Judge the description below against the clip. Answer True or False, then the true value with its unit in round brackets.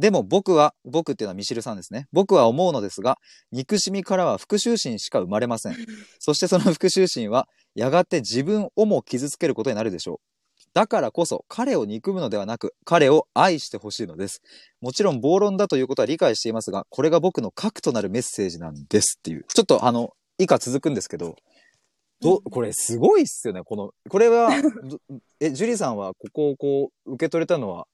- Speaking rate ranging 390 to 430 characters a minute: True (410 characters per minute)